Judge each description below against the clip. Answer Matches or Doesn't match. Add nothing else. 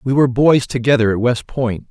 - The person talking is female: Doesn't match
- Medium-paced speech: Doesn't match